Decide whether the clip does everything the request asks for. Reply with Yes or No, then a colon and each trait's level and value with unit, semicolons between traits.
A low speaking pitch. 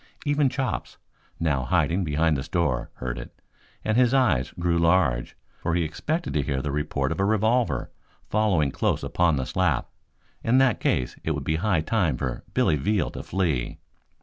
Yes: very low, 85 Hz